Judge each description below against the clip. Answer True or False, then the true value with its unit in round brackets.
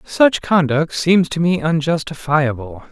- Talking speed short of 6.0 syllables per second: True (4.0 syllables/s)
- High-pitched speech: False (160 Hz)